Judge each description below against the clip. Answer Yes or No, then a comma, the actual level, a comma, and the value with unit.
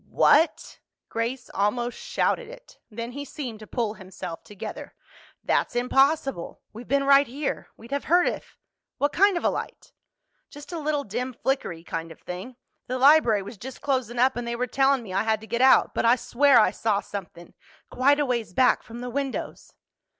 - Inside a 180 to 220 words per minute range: Yes, average, 185 wpm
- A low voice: No, very high, 250 Hz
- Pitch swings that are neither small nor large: Yes, average, 4.1 semitones